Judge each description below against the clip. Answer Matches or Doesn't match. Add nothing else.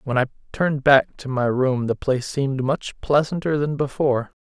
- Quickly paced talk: Doesn't match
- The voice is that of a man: Matches